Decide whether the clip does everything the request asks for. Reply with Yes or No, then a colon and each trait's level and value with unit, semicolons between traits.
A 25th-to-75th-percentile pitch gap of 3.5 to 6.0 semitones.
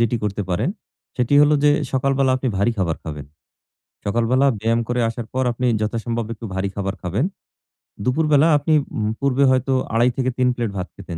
Yes: average, 4.1 semitones